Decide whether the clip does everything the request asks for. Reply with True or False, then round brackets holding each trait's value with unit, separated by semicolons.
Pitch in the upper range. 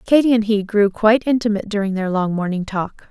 True (210 Hz)